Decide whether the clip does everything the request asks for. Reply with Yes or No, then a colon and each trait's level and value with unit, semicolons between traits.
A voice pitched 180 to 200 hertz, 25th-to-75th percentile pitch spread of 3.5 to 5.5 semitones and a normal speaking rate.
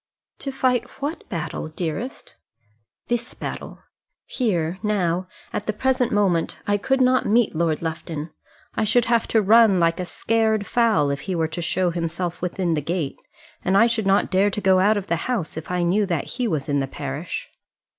Yes: high, 190 Hz; average, 5.1 semitones; average, 190 wpm